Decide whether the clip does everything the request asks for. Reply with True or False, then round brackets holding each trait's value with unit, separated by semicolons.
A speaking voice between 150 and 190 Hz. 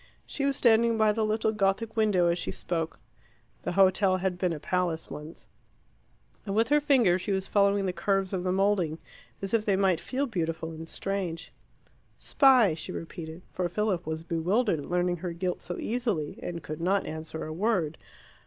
True (185 Hz)